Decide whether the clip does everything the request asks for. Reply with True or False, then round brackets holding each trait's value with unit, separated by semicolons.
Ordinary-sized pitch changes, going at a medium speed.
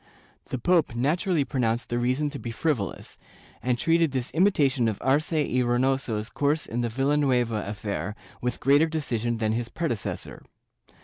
True (4.0 semitones; 160 wpm)